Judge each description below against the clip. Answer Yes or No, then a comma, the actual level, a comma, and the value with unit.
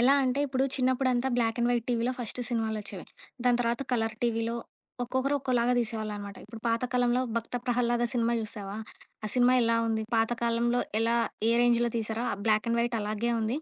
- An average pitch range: No, narrow, 1.6 semitones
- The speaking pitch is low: No, high, 235 Hz